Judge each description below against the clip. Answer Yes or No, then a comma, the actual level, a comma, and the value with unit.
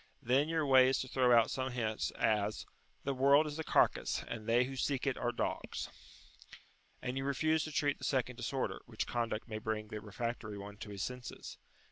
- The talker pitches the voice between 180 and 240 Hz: No, low, 125 Hz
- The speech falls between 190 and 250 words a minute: Yes, fast, 205 wpm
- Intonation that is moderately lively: Yes, average, 3.6 semitones